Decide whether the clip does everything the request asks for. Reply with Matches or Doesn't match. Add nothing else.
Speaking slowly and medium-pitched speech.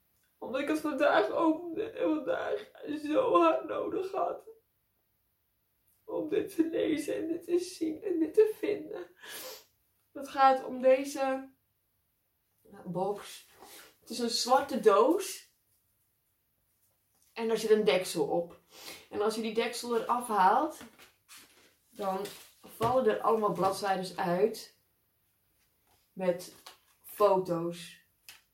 Doesn't match